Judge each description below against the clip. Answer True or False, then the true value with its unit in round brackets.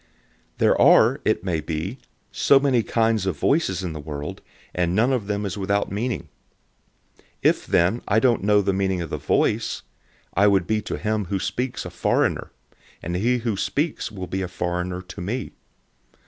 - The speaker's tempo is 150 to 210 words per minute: True (190 wpm)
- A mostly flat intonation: False (4.0 semitones)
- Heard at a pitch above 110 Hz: False (100 Hz)